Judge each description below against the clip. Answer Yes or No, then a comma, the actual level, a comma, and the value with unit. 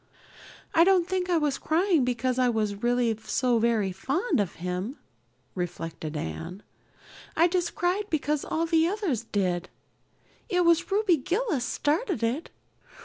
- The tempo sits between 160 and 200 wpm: No, average, 145 wpm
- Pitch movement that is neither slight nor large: No, wide, 8.3 semitones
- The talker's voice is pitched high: Yes, very high, 275 Hz